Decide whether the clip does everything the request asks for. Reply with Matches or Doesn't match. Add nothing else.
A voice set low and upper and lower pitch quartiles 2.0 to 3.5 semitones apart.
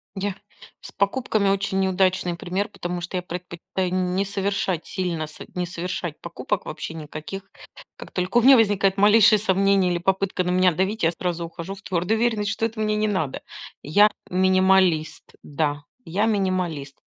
Doesn't match